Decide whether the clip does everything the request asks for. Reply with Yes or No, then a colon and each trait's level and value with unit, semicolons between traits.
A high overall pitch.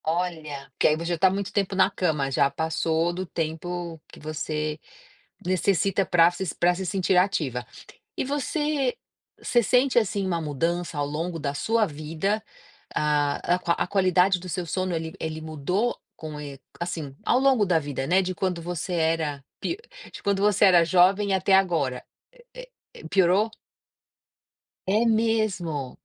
No: medium, 175 Hz